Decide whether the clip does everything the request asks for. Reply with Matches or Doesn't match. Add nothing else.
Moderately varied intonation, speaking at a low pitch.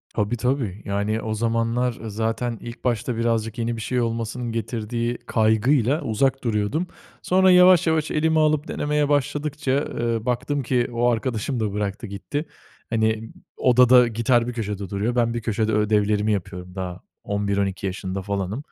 Matches